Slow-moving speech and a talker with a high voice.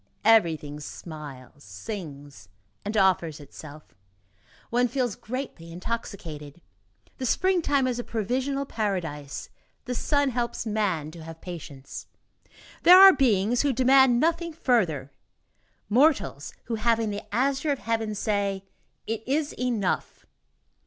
Yes: slow, 120 wpm; high, 215 Hz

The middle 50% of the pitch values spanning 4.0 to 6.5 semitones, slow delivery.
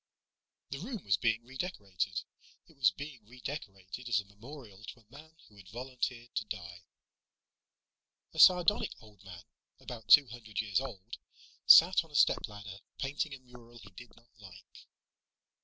No: average, 5.2 semitones; average, 155 wpm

